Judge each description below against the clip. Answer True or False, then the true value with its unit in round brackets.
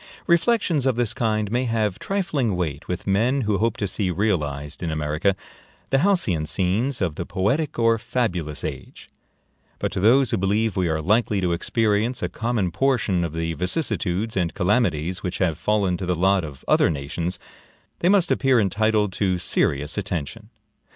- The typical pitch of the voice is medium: False (100 Hz)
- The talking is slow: False (170 wpm)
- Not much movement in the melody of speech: False (5.1 semitones)